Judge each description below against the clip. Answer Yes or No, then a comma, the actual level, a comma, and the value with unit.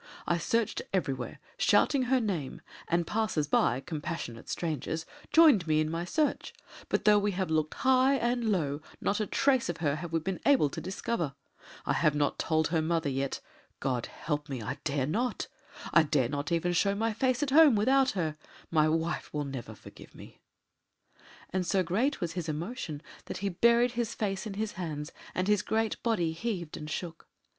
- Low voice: No, medium, 175 Hz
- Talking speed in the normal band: Yes, average, 190 wpm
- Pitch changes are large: Yes, wide, 6.3 semitones